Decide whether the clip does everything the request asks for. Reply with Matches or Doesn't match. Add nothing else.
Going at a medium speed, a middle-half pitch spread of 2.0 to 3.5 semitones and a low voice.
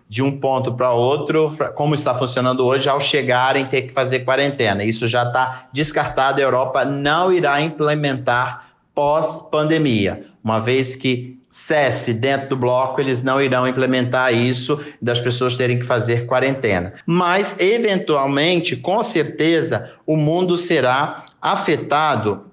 Matches